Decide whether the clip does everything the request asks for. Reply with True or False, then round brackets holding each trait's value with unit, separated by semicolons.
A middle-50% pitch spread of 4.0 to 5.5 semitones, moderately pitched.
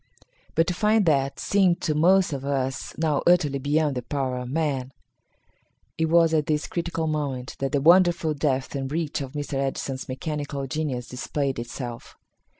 False (3.3 semitones; 145 Hz)